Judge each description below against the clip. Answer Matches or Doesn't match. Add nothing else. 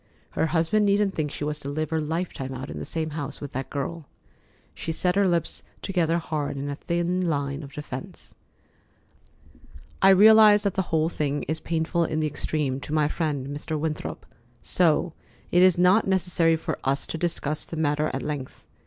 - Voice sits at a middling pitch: Matches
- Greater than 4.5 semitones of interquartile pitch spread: Doesn't match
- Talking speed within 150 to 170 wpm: Doesn't match